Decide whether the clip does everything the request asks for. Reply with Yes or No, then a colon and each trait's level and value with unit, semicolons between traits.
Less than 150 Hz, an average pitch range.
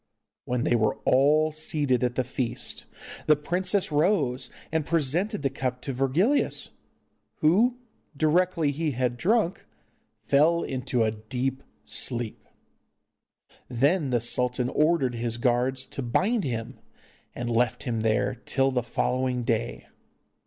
Yes: low, 135 Hz; average, 4.2 semitones